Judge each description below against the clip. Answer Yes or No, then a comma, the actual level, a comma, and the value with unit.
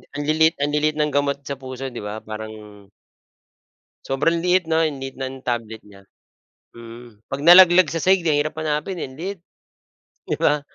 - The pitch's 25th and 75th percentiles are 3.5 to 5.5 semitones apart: Yes, average, 4.0 semitones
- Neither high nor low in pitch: Yes, medium, 145 Hz